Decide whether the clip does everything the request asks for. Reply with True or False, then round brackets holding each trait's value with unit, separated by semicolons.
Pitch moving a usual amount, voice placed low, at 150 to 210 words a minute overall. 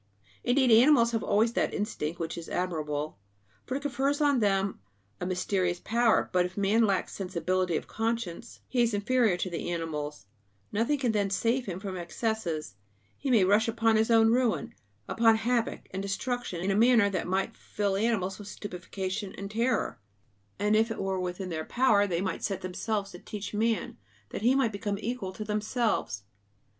False (3.9 semitones; 205 Hz; 180 wpm)